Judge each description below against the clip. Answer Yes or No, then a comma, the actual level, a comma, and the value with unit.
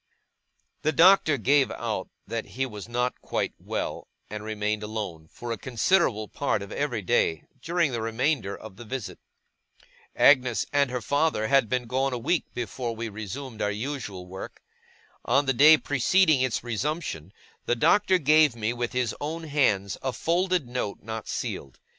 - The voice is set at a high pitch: No, low, 125 Hz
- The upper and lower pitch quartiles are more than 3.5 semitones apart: Yes, average, 4.8 semitones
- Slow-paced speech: No, average, 165 wpm